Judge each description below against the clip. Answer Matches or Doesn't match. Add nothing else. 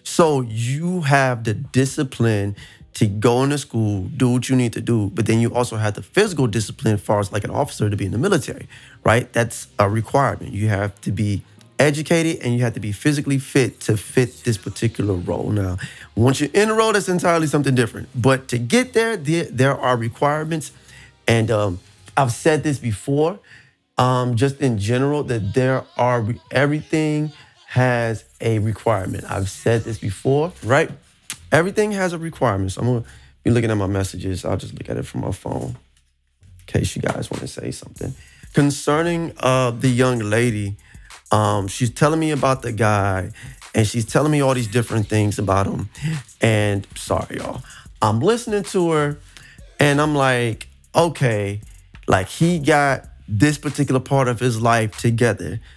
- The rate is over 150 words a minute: Matches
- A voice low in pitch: Matches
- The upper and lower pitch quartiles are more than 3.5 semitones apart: Matches